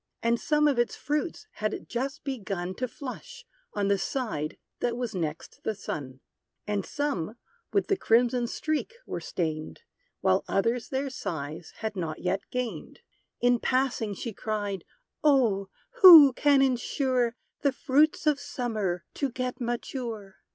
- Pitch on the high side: Yes, high, 240 Hz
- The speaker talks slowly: No, average, 145 wpm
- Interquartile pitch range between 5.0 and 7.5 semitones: Yes, wide, 5.6 semitones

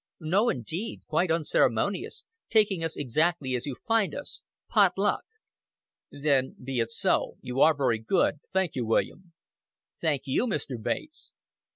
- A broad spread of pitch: Yes, wide, 6.4 semitones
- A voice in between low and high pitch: Yes, medium, 155 Hz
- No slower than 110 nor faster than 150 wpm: Yes, average, 145 wpm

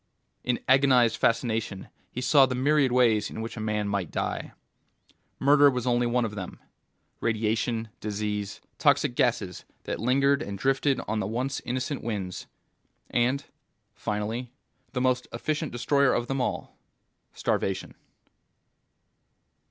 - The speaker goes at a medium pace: No, slow, 130 wpm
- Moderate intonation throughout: Yes, average, 3.6 semitones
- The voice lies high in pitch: No, low, 120 Hz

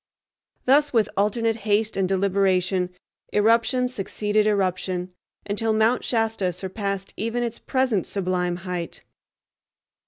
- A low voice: No, high, 205 Hz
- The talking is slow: Yes, slow, 105 wpm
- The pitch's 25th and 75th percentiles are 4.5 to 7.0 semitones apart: No, average, 3.2 semitones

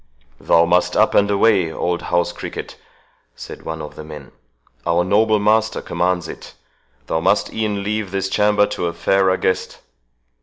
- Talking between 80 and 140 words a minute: No, average, 155 wpm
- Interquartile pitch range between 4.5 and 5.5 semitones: No, average, 3.1 semitones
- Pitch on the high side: No, very low, 95 Hz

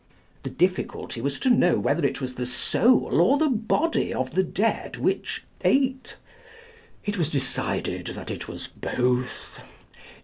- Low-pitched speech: No, medium, 175 Hz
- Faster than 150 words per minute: No, average, 145 wpm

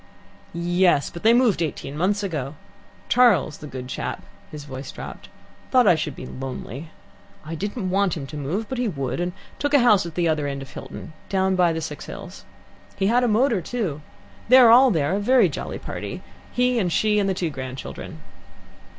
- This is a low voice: No, medium, 180 Hz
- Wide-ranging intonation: Yes, wide, 6.6 semitones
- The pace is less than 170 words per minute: No, average, 200 wpm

